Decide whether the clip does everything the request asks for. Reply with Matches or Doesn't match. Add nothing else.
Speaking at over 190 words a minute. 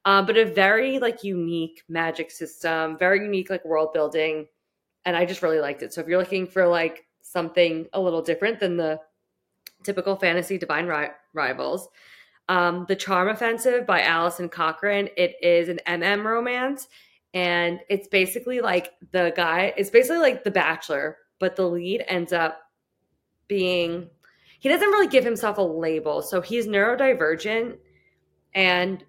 Doesn't match